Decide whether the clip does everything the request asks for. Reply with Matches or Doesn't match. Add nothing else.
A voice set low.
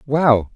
Matches